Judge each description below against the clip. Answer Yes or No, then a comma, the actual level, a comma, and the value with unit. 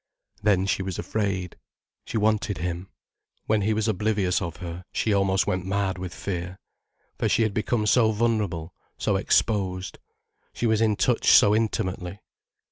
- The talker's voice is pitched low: Yes, low, 100 Hz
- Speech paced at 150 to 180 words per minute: Yes, average, 155 wpm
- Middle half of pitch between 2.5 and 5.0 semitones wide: Yes, average, 2.8 semitones